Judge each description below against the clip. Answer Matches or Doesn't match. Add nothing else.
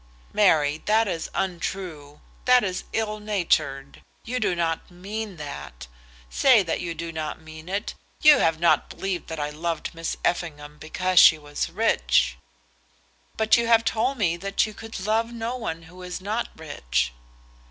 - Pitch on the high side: Doesn't match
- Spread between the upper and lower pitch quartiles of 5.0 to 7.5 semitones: Matches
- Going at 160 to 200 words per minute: Matches